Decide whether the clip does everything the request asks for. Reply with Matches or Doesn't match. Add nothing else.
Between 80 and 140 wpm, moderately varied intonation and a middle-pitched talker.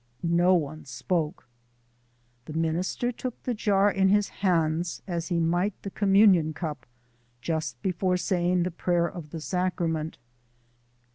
Matches